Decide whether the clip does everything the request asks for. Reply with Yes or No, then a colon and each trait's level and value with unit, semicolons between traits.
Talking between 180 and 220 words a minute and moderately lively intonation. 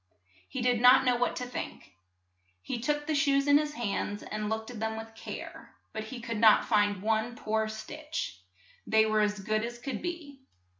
Yes: average, 195 wpm; average, 3.8 semitones